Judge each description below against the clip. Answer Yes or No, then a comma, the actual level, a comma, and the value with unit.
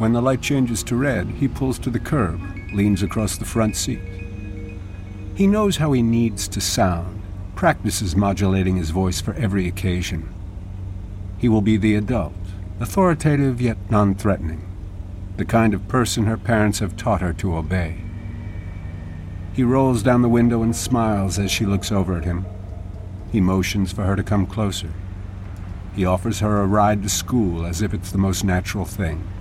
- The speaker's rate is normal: Yes, average, 170 wpm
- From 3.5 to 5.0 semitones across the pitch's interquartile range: No, average, 3.1 semitones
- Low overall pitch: Yes, low, 100 Hz